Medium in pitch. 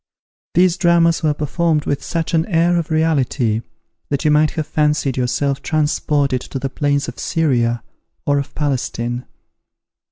Yes: medium, 150 Hz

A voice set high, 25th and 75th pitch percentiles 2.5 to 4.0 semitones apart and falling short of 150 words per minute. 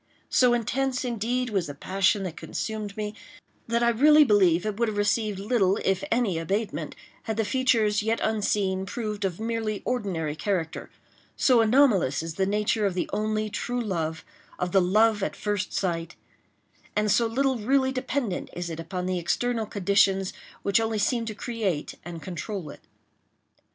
No: high, 210 Hz; average, 3.4 semitones; average, 160 wpm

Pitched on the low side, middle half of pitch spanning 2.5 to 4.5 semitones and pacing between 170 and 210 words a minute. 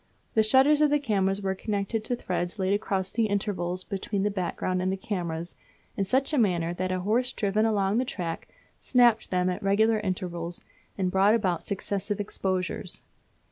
No: high, 195 Hz; average, 2.9 semitones; average, 180 wpm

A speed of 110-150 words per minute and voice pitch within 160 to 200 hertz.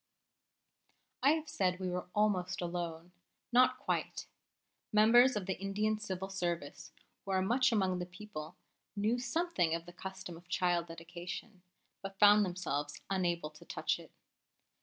Yes: average, 145 wpm; medium, 185 Hz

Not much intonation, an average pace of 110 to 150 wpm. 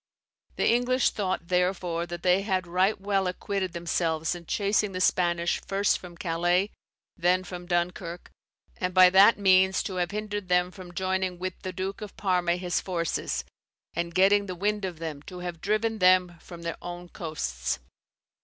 No: narrow, 1.8 semitones; average, 175 wpm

